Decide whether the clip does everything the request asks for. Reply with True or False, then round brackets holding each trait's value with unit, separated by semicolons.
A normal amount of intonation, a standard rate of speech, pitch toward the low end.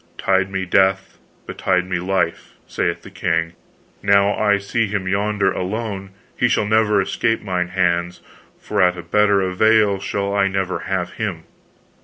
False (2.1 semitones; 155 wpm; 95 Hz)